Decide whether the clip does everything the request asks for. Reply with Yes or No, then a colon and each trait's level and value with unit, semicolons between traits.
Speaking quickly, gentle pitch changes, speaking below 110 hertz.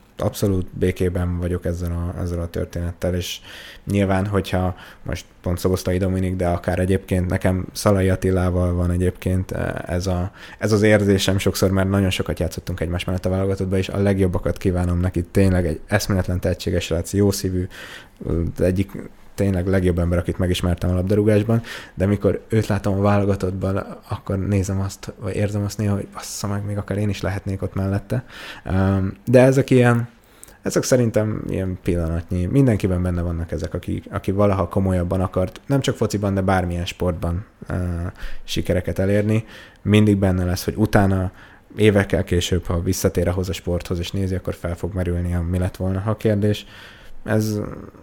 Yes: fast, 165 wpm; narrow, 2.3 semitones; very low, 95 Hz